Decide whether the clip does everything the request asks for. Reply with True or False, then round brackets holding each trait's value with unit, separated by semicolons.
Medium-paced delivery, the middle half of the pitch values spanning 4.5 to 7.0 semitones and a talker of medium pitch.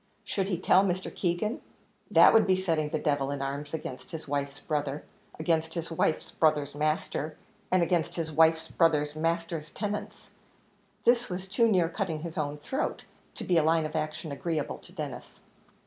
False (175 wpm; 2.9 semitones; 160 Hz)